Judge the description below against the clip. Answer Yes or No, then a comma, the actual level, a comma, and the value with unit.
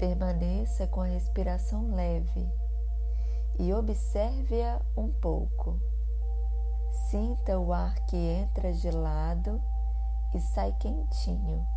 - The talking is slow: Yes, slow, 95 wpm